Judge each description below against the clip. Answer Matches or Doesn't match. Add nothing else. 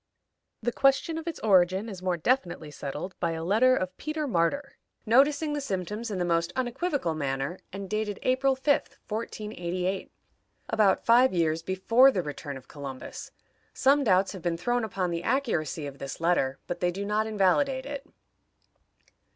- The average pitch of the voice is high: Matches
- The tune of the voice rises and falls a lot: Matches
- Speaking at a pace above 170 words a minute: Doesn't match